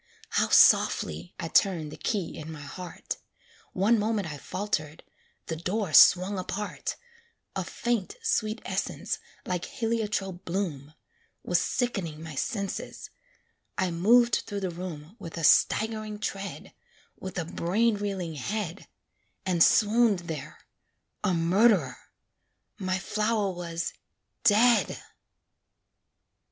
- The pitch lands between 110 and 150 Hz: No, high, 190 Hz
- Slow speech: Yes, slow, 115 wpm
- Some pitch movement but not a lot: Yes, average, 4.1 semitones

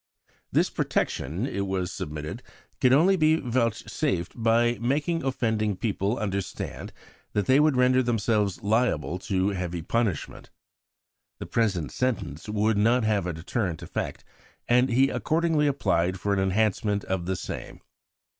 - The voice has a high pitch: No, low, 110 Hz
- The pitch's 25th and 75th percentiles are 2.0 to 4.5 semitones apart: No, average, 5.0 semitones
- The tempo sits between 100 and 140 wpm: Yes, slow, 135 wpm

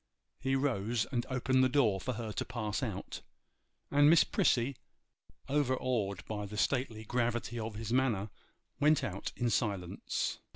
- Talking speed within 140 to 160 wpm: Yes, average, 150 wpm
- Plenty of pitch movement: No, average, 3.5 semitones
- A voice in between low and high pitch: No, low, 120 Hz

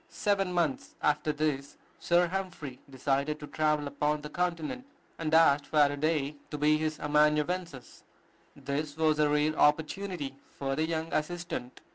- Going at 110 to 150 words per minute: Yes, average, 140 wpm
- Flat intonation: Yes, narrow, 2.0 semitones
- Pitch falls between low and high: Yes, medium, 150 Hz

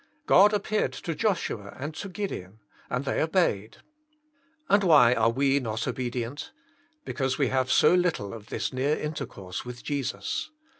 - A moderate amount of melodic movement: No, wide, 6.1 semitones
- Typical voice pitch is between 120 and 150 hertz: Yes, low, 135 Hz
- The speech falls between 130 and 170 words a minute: Yes, average, 155 wpm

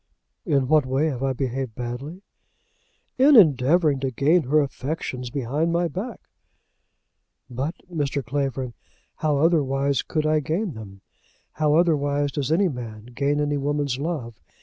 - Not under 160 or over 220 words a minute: No, average, 140 wpm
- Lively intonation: No, average, 3.2 semitones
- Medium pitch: Yes, medium, 145 Hz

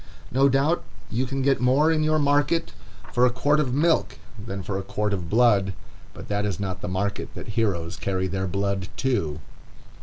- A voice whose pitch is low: Yes, low, 115 Hz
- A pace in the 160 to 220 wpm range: Yes, average, 190 wpm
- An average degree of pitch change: No, wide, 6.0 semitones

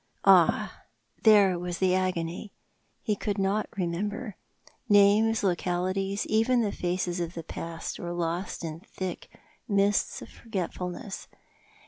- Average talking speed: No, slow, 125 wpm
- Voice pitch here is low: No, high, 190 Hz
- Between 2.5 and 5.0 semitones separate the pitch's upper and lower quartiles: Yes, average, 2.8 semitones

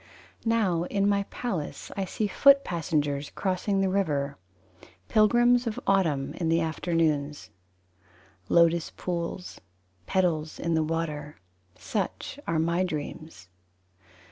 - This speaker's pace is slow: Yes, slow, 115 wpm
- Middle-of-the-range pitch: Yes, medium, 170 Hz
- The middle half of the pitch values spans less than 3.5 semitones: No, average, 4.0 semitones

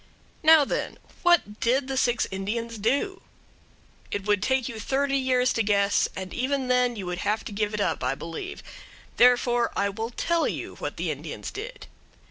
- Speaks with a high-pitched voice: Yes, high, 240 Hz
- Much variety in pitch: No, average, 4.5 semitones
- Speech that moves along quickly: No, average, 180 wpm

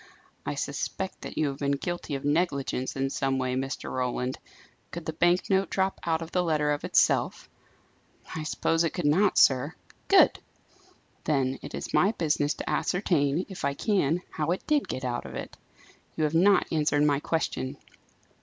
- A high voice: No, medium, 155 Hz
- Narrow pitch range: No, average, 4.2 semitones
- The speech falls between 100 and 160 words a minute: No, average, 180 wpm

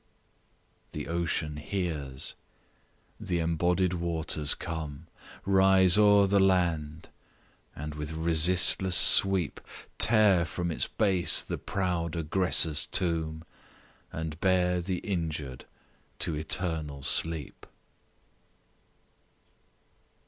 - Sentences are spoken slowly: Yes, slow, 90 wpm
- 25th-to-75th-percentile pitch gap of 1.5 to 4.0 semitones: Yes, average, 2.9 semitones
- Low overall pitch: Yes, very low, 85 Hz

